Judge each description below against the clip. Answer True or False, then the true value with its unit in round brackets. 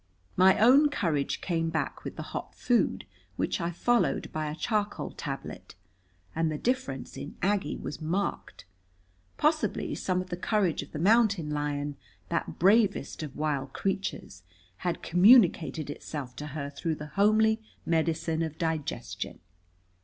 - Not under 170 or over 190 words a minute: False (145 wpm)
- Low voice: False (165 Hz)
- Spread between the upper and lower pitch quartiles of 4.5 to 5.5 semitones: True (5.2 semitones)